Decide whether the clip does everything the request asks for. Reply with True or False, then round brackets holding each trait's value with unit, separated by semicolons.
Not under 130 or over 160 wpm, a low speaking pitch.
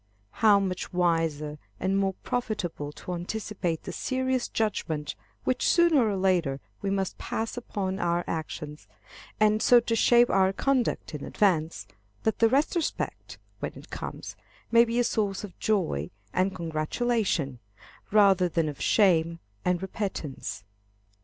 False (140 wpm; 190 Hz)